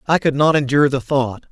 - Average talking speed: No, fast, 235 wpm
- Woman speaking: No, male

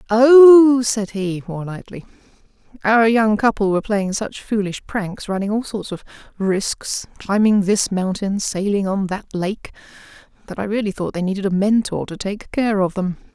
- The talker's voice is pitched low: No, high, 205 Hz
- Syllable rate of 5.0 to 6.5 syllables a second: No, 4.5 syllables/s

